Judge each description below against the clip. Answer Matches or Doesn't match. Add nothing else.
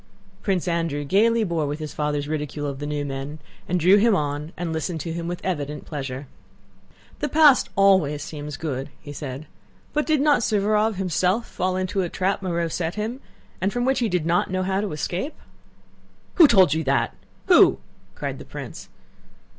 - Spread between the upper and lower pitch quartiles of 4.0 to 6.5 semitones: Matches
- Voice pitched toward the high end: Doesn't match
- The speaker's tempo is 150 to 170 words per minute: Doesn't match